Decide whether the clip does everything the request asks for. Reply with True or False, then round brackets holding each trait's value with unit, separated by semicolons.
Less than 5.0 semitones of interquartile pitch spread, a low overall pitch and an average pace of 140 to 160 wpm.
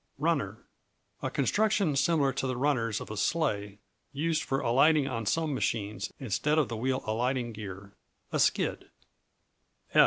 False (5.6 semitones; 130 Hz; 145 wpm)